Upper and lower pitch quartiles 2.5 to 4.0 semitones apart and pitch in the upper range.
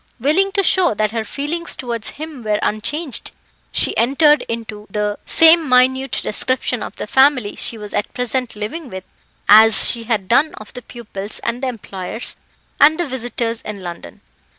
No: average, 4.8 semitones; high, 240 Hz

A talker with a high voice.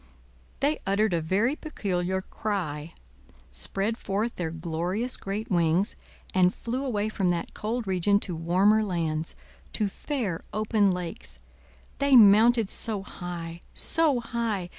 Yes: high, 200 Hz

